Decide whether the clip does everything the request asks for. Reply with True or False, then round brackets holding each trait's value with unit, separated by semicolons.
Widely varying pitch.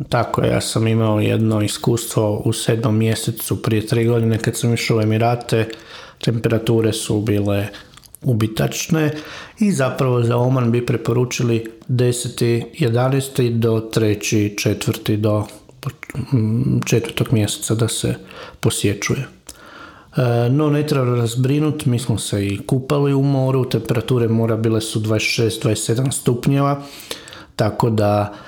False (2.6 semitones)